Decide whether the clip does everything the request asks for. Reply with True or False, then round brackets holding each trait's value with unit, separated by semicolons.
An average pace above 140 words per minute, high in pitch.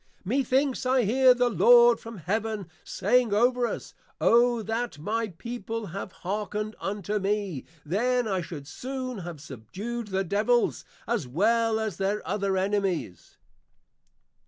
False (135 wpm; 215 Hz)